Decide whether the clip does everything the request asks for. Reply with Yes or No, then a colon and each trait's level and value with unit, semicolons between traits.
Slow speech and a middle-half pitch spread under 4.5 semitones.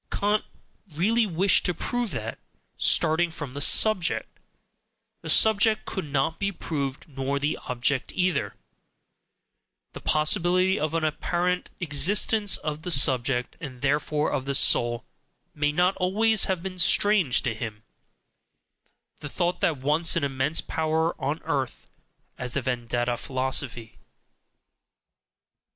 No: slow, 130 wpm; average, 5.2 semitones